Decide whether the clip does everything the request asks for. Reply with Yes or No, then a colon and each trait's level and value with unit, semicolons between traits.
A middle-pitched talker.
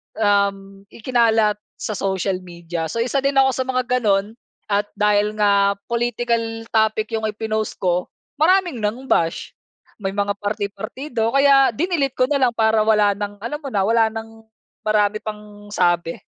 No: high, 215 Hz